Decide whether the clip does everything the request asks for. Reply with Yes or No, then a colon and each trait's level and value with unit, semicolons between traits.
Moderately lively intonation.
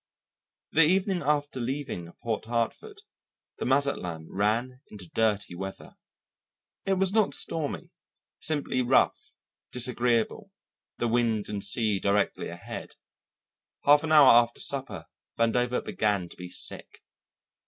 No: wide, 5.7 semitones